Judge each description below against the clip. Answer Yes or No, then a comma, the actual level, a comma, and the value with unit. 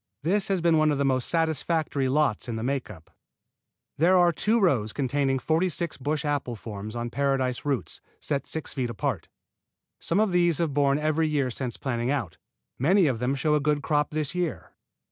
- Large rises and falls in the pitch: No, average, 3.8 semitones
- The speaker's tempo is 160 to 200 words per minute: Yes, average, 195 wpm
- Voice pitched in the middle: Yes, medium, 145 Hz